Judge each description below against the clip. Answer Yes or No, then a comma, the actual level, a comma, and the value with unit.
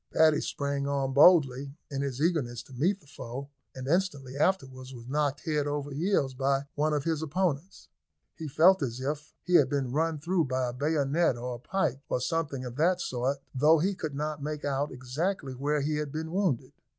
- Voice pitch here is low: No, medium, 145 Hz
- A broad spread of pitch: No, average, 3.1 semitones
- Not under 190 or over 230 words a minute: Yes, average, 200 wpm